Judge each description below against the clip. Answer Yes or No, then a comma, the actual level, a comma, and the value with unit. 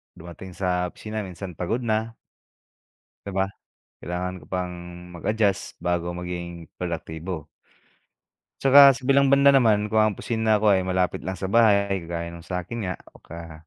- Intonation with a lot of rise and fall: No, average, 3.8 semitones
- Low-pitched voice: Yes, very low, 95 Hz